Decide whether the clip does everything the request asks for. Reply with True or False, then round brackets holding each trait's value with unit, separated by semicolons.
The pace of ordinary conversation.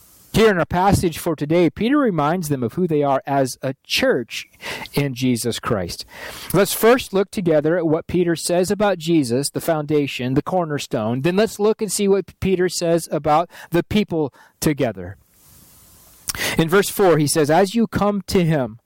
True (175 wpm)